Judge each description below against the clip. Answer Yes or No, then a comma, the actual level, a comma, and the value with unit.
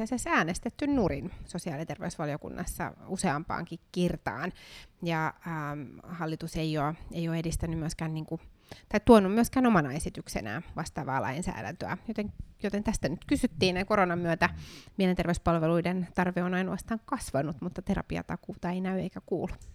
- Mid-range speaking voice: Yes, medium, 175 Hz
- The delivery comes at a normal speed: Yes, average, 130 wpm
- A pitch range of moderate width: Yes, average, 3.0 semitones